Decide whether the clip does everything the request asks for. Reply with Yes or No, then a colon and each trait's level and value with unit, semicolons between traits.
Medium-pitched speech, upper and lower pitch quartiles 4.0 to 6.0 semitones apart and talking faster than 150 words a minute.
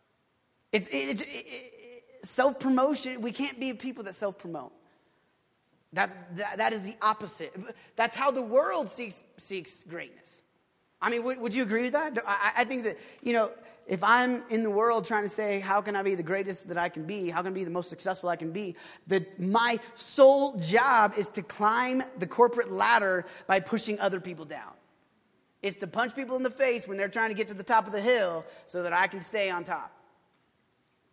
No: high, 215 Hz; average, 4.4 semitones; average, 200 wpm